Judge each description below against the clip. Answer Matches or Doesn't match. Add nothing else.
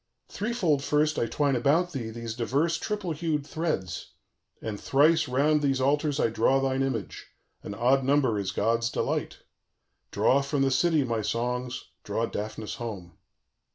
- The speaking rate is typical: Matches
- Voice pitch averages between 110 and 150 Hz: Matches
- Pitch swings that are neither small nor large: Matches